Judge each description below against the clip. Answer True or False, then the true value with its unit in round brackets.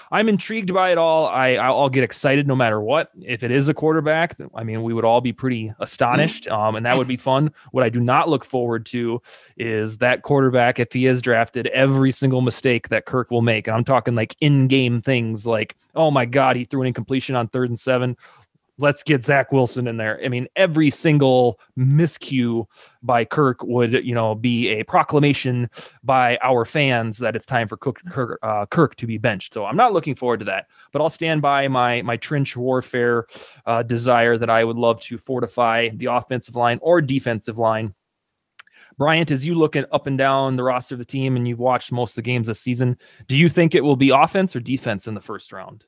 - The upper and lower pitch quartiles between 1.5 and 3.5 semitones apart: True (2.5 semitones)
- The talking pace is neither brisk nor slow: False (220 wpm)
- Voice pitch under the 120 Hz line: False (125 Hz)